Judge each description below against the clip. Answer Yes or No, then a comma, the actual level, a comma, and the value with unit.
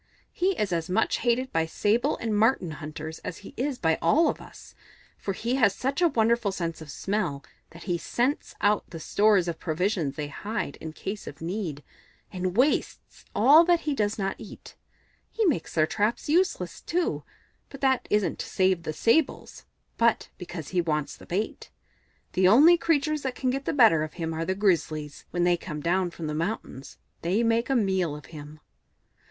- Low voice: No, high, 195 Hz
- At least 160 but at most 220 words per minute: Yes, average, 190 wpm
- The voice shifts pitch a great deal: Yes, wide, 6.6 semitones